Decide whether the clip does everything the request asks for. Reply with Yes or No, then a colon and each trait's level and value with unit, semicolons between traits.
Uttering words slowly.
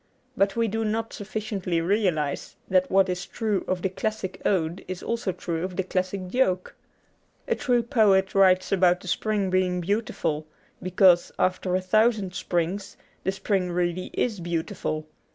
No: average, 155 wpm